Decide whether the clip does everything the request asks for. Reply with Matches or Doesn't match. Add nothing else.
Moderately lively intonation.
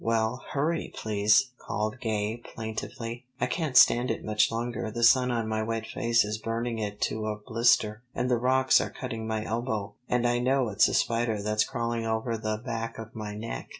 Doesn't match